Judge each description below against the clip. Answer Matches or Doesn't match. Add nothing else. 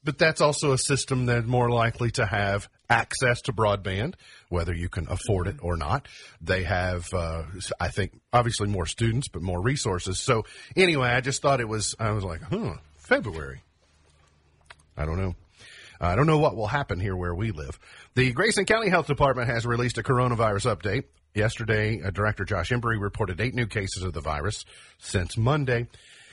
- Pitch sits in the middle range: Doesn't match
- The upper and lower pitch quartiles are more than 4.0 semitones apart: Matches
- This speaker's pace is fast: Doesn't match